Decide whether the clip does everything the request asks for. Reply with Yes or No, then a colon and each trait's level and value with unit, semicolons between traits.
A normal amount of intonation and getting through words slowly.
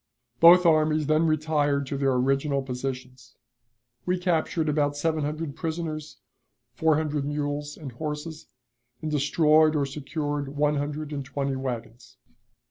No: narrow, 2.1 semitones; slow, 130 wpm